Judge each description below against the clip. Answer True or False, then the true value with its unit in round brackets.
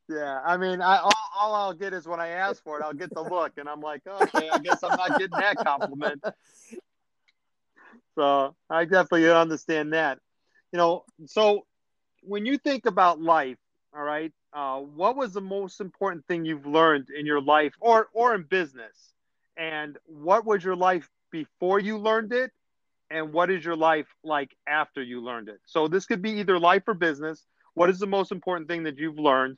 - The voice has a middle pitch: True (170 Hz)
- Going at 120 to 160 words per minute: False (195 wpm)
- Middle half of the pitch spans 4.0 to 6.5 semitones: True (4.5 semitones)